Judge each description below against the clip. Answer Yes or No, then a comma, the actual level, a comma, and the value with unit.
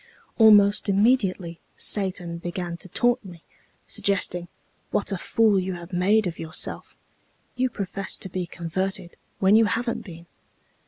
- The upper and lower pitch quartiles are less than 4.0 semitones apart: Yes, average, 3.1 semitones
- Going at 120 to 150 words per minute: Yes, average, 140 wpm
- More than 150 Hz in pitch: Yes, high, 190 Hz